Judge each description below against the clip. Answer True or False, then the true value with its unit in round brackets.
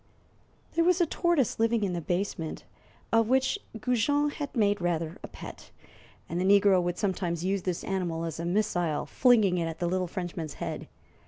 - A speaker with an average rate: True (180 wpm)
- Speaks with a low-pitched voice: False (190 Hz)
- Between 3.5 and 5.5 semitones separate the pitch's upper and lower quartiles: True (4.7 semitones)